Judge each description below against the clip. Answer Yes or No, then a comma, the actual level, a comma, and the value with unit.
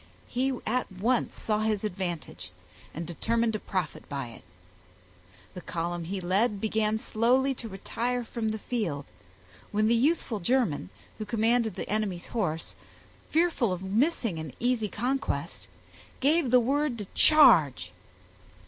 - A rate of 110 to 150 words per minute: Yes, average, 140 wpm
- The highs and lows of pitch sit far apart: No, average, 4.8 semitones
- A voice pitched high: Yes, high, 220 Hz